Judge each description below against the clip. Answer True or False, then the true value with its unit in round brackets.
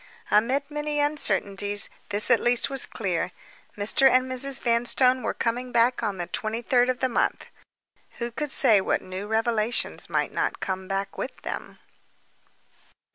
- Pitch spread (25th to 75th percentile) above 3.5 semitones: True (4.0 semitones)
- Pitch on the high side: True (235 Hz)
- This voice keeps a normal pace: True (155 wpm)